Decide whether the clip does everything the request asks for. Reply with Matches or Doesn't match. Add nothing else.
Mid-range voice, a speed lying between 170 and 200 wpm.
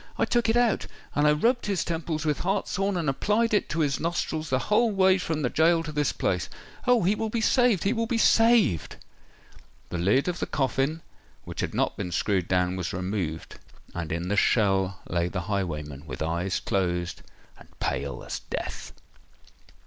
Matches